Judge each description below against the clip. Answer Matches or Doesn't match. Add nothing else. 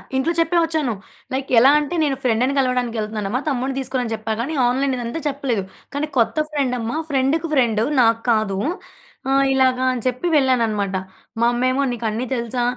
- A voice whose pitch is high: Matches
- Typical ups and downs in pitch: Matches